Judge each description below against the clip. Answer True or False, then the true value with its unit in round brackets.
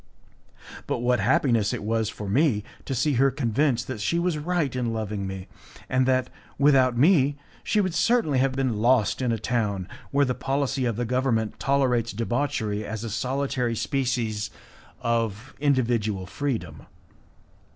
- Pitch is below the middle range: True (125 Hz)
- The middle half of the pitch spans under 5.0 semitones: True (3.7 semitones)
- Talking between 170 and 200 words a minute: False (155 wpm)